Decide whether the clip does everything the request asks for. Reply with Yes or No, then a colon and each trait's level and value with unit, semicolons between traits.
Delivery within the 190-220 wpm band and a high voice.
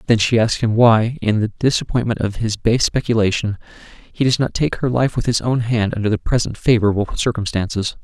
No: average, 200 wpm; low, 110 Hz